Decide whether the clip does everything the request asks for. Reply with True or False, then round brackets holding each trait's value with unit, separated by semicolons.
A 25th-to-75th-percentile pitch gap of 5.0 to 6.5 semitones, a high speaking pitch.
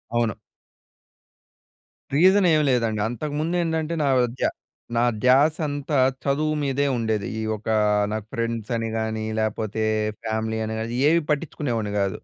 False (5.3 semitones; 120 Hz)